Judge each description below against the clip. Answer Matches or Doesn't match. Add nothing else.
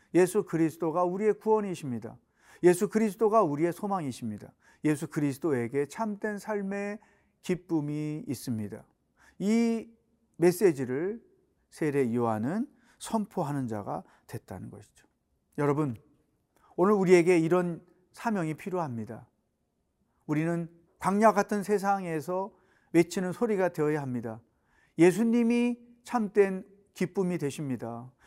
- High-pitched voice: Doesn't match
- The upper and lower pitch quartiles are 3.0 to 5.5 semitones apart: Doesn't match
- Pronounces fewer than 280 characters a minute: Matches